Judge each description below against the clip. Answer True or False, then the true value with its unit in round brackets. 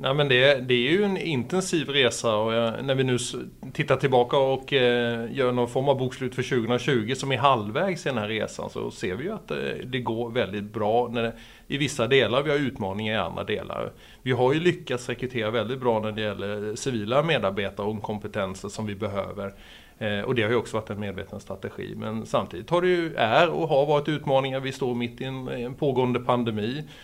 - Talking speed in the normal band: False (205 wpm)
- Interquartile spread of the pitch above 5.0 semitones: False (3.7 semitones)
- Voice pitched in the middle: False (125 Hz)